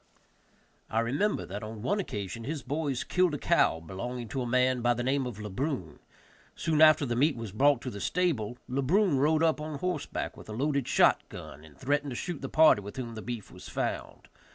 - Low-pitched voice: Yes, low, 130 Hz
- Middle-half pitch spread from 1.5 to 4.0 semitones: No, average, 5.0 semitones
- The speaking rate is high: Yes, fast, 220 wpm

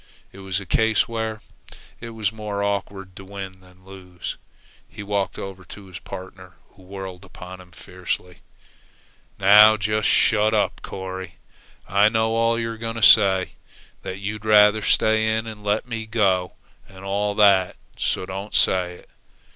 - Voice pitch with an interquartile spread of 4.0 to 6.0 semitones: No, narrow, 2.5 semitones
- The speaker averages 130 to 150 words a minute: No, average, 165 wpm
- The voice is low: Yes, low, 100 Hz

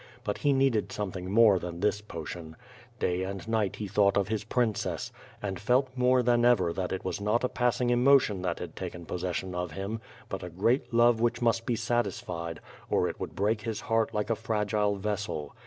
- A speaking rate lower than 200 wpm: No, fast, 205 wpm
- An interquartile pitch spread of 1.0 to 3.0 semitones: No, average, 4.0 semitones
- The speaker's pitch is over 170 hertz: No, low, 105 Hz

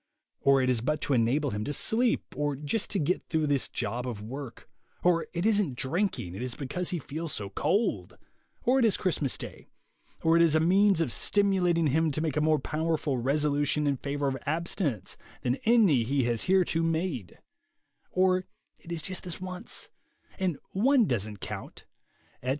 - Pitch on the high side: No, medium, 155 Hz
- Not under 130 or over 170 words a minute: No, average, 185 wpm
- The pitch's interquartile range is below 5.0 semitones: No, wide, 5.4 semitones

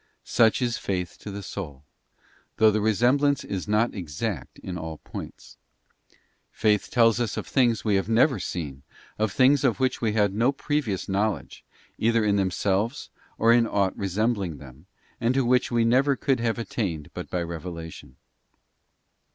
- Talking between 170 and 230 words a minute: No, average, 160 wpm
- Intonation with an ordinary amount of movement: Yes, average, 4.1 semitones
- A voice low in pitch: Yes, low, 110 Hz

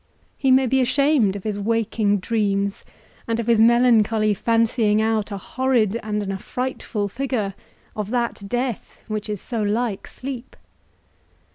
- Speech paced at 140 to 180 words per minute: Yes, average, 145 wpm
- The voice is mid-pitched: No, high, 225 Hz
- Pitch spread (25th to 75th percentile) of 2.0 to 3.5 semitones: Yes, average, 2.8 semitones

